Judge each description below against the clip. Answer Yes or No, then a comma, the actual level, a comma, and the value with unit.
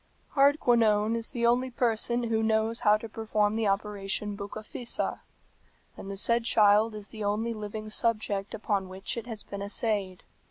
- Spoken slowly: No, average, 165 wpm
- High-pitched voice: Yes, high, 215 Hz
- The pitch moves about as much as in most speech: No, narrow, 2.0 semitones